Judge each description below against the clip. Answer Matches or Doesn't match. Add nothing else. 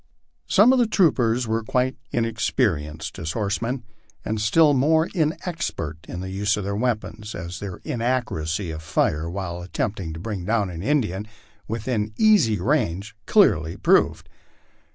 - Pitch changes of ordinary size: Doesn't match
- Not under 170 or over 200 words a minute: Doesn't match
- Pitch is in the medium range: Doesn't match